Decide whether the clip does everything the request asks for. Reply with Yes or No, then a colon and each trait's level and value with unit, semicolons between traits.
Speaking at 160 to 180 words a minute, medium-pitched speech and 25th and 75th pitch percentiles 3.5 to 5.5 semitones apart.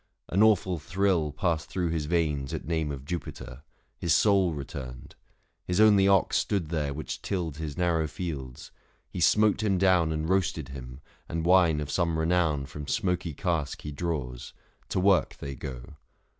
No: average, 170 wpm; very low, 80 Hz; average, 3.8 semitones